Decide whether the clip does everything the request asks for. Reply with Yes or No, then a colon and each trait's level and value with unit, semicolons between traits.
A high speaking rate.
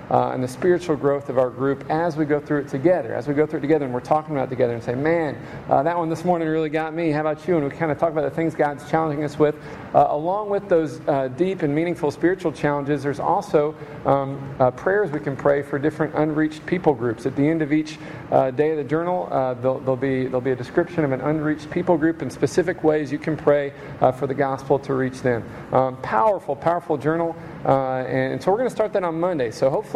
Yes: fast, 255 wpm